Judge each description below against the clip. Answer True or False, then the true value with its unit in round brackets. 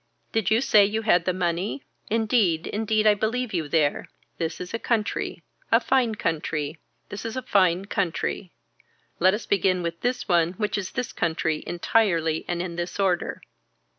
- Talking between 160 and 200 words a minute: True (170 wpm)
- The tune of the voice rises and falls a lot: False (4.4 semitones)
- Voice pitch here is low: False (190 Hz)